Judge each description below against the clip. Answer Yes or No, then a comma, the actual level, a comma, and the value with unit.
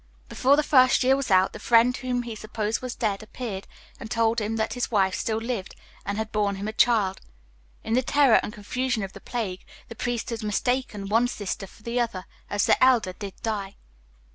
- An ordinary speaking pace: No, fast, 210 wpm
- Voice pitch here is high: Yes, high, 225 Hz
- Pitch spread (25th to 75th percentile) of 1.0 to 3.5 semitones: Yes, average, 3.2 semitones